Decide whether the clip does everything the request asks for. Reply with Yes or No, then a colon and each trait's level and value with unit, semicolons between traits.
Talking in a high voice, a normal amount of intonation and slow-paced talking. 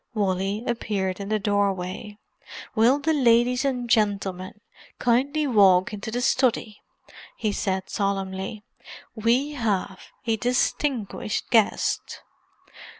Yes: high, 215 Hz; average, 3.8 semitones; slow, 105 wpm